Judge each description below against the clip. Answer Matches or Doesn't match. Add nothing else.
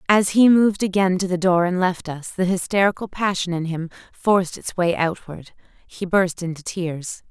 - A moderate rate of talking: Matches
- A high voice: Doesn't match